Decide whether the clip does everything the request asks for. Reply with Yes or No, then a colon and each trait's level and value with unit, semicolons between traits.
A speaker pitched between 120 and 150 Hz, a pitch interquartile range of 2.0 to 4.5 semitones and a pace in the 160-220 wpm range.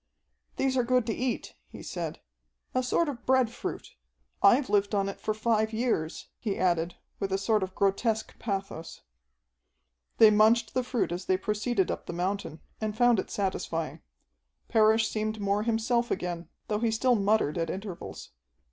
No: high, 215 Hz; average, 3.4 semitones; average, 165 wpm